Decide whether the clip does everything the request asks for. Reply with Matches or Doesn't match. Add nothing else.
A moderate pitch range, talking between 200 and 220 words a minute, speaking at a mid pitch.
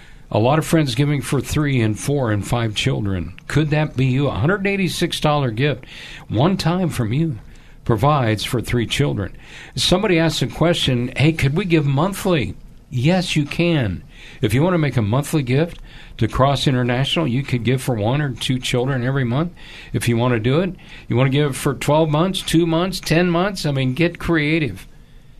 Matches